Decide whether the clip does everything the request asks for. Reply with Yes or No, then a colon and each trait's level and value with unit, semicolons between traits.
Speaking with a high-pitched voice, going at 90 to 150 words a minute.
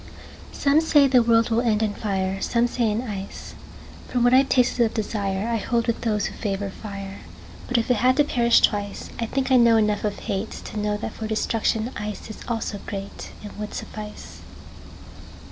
No: high, 220 Hz; average, 165 wpm